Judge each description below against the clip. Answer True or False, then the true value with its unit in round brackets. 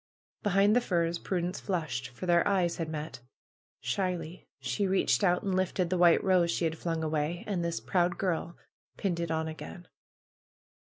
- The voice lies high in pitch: False (175 Hz)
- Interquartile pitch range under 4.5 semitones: True (2.5 semitones)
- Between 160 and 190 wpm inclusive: True (170 wpm)